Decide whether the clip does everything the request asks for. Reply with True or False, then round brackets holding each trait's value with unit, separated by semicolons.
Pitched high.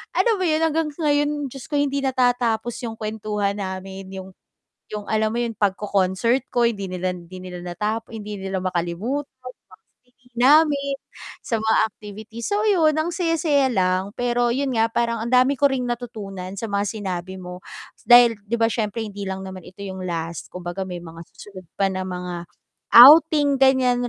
True (225 Hz)